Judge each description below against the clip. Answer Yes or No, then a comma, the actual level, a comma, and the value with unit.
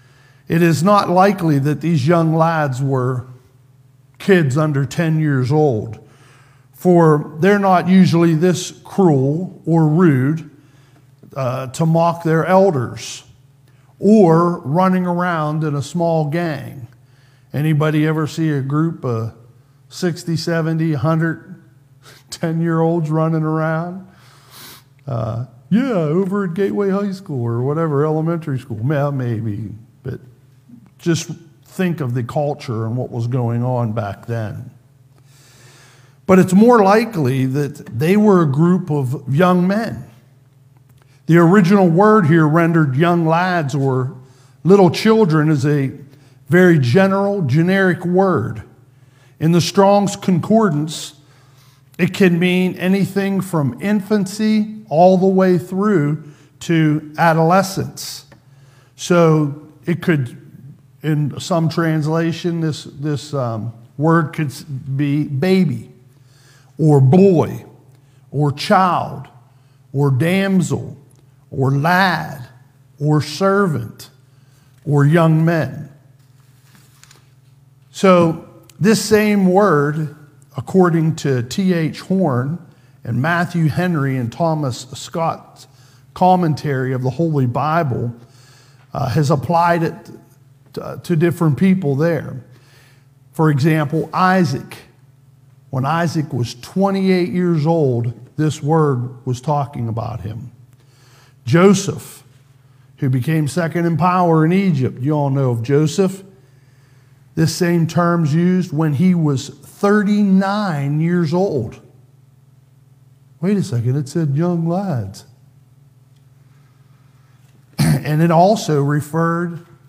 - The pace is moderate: No, slow, 110 wpm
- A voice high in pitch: No, medium, 150 Hz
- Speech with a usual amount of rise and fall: Yes, average, 4.3 semitones